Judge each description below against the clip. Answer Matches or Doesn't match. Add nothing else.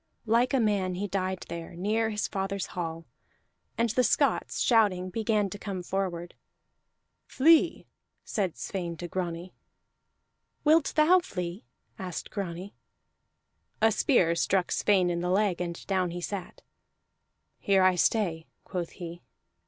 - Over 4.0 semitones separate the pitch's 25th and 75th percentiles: Doesn't match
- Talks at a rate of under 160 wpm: Matches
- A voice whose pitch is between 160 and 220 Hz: Matches